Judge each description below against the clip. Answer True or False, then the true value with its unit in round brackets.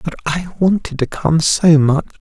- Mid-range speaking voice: True (160 Hz)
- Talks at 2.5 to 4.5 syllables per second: True (4.3 syllables/s)